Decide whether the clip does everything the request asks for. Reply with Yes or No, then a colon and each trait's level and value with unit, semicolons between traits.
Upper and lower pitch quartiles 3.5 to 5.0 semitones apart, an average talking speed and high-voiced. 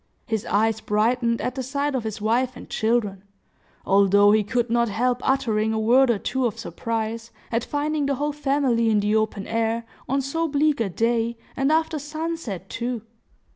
Yes: average, 3.8 semitones; average, 180 wpm; high, 235 Hz